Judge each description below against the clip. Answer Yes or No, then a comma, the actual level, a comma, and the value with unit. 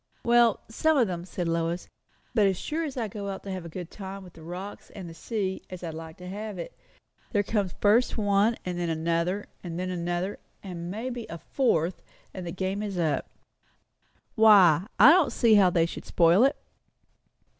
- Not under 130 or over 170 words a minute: No, average, 200 wpm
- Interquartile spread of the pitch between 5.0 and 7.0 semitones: No, average, 3.7 semitones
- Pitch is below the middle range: No, high, 190 Hz